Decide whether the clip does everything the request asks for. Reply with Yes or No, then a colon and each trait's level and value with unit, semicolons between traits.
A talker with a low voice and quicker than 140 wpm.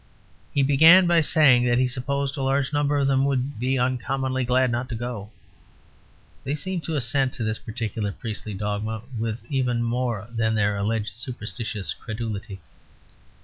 Yes: low, 125 Hz; average, 160 wpm